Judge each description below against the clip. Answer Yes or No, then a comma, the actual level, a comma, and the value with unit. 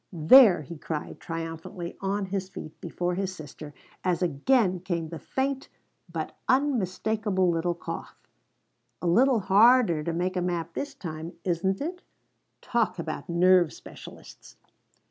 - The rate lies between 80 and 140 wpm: Yes, slow, 135 wpm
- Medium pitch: Yes, medium, 180 Hz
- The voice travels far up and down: No, average, 3.6 semitones